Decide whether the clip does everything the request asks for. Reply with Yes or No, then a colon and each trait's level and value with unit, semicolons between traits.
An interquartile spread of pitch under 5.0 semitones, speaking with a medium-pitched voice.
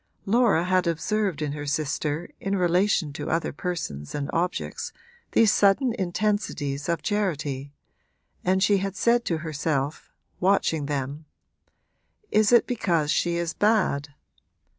No: average, 5.3 semitones; medium, 170 Hz